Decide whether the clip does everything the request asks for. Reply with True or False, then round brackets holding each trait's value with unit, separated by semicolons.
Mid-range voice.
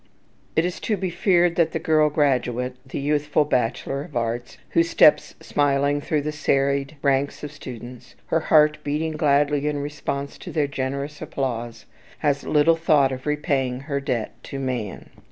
True (145 Hz)